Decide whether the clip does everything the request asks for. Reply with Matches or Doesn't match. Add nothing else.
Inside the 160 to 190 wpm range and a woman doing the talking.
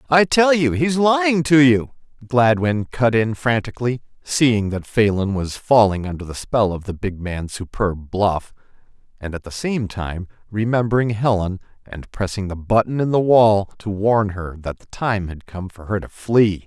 Doesn't match